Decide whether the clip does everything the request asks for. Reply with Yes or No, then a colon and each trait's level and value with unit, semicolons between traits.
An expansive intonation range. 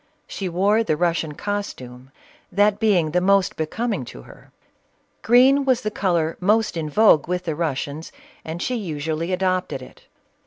No: average, 4.8 semitones